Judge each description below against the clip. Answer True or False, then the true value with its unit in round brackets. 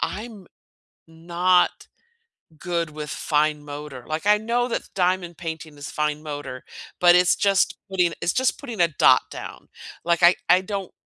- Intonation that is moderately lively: True (3.7 semitones)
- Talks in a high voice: False (175 Hz)